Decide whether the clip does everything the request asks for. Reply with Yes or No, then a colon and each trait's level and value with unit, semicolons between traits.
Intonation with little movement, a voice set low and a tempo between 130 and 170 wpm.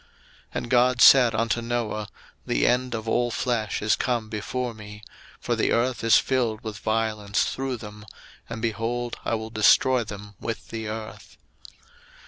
Yes: narrow, 2.1 semitones; low, 115 Hz; average, 160 wpm